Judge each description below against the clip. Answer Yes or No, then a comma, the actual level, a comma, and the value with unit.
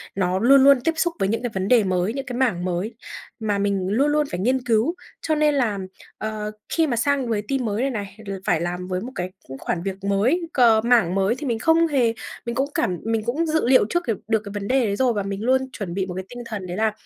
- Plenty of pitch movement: No, average, 5.0 semitones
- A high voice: Yes, high, 225 Hz